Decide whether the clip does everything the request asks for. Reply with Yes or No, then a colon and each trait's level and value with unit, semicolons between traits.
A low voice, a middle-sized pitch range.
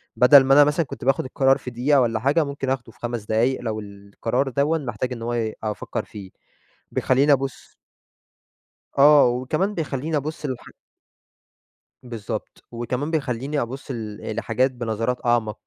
Yes: low, 125 Hz; average, 3.4 semitones